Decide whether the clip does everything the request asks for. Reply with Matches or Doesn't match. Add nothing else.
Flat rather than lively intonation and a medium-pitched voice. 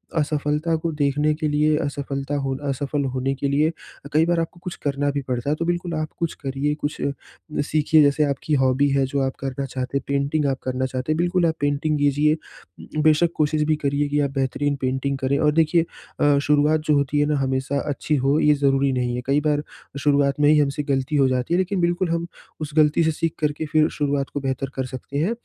Matches